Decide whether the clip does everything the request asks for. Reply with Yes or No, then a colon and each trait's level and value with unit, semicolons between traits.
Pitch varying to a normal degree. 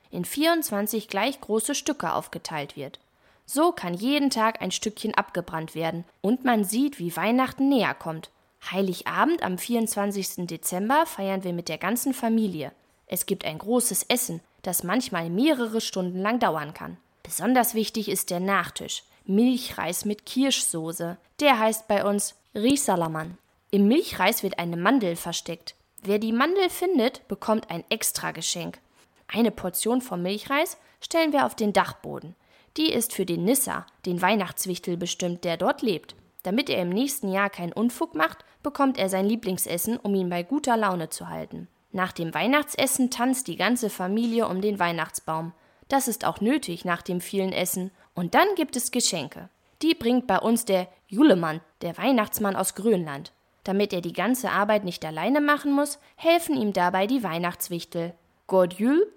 No: wide, 5.7 semitones